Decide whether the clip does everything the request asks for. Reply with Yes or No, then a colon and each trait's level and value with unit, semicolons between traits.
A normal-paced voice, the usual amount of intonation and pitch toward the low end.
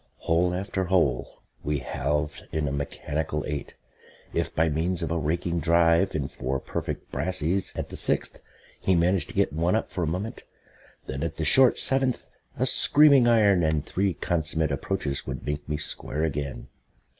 Yes: average, 170 wpm; average, 3.7 semitones; very low, 80 Hz